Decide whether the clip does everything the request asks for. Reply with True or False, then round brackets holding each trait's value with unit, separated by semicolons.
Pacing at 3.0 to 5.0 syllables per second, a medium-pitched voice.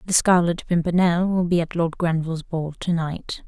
True (4.9 syllables/s; 170 Hz)